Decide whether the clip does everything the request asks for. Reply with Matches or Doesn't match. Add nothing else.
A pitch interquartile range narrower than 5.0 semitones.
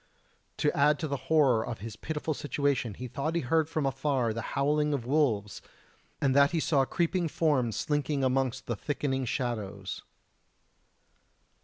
Matches